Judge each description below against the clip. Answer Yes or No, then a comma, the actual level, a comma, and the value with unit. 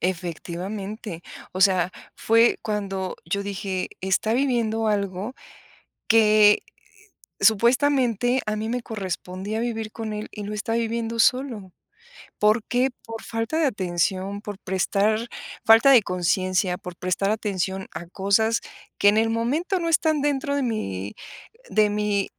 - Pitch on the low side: No, high, 215 Hz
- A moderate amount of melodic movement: Yes, average, 3.3 semitones